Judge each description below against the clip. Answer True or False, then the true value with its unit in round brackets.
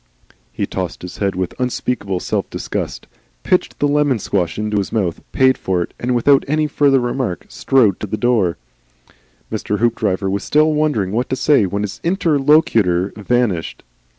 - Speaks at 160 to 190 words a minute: True (165 wpm)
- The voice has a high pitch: False (115 Hz)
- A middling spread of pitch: False (5.8 semitones)